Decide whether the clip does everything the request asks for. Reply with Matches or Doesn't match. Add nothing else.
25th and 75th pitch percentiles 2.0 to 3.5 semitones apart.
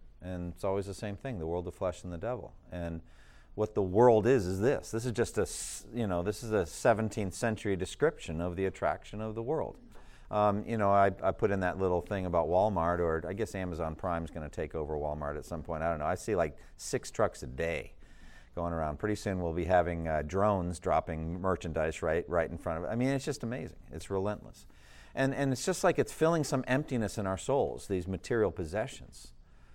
Doesn't match